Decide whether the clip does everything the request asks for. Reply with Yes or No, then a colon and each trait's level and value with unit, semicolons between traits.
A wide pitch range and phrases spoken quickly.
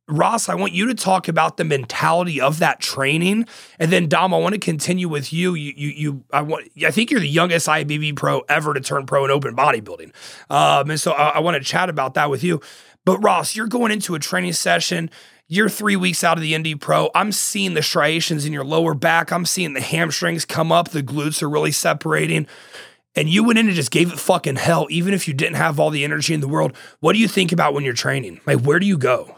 No: average, 3.7 semitones; fast, 245 wpm